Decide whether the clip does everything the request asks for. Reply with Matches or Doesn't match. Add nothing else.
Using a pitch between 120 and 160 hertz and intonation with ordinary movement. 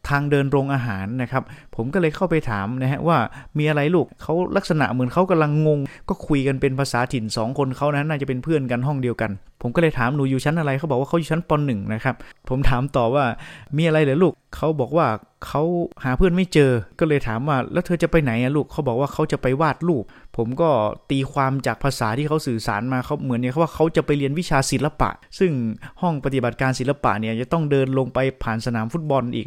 Matches